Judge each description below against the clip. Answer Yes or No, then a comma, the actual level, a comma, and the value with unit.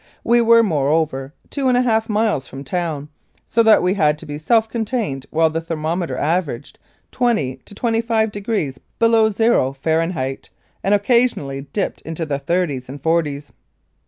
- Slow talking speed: No, average, 160 wpm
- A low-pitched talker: No, medium, 165 Hz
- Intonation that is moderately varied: No, wide, 7.5 semitones